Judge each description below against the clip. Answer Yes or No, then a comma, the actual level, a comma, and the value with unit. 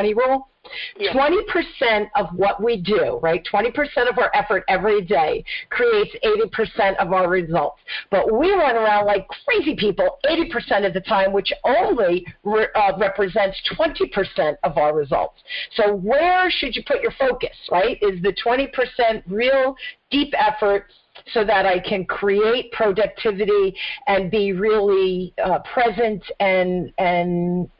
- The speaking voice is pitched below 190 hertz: No, high, 220 Hz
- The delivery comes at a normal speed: Yes, average, 155 wpm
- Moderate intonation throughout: No, wide, 6.4 semitones